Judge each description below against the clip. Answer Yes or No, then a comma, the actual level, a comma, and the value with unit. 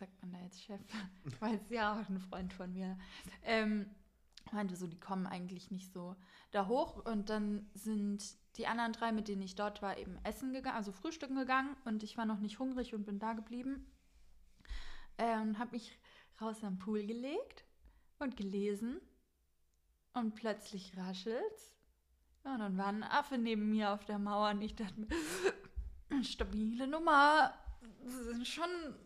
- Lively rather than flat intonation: No, average, 3.3 semitones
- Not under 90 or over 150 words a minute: No, average, 165 wpm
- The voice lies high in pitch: Yes, high, 215 Hz